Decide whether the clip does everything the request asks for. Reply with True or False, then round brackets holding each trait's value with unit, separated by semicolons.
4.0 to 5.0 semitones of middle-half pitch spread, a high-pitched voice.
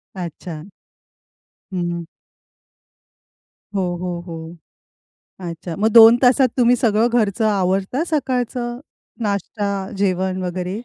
True (4.7 semitones; 200 Hz)